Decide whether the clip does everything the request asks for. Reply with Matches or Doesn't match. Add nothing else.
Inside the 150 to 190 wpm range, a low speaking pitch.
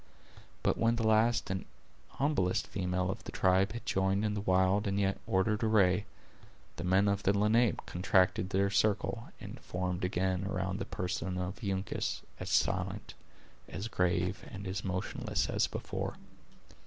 Matches